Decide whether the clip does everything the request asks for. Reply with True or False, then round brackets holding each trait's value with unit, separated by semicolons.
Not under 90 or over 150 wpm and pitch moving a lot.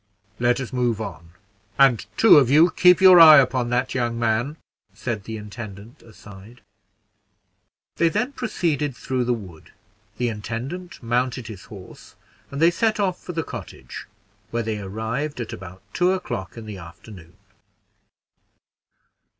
True (145 wpm; 5.9 semitones)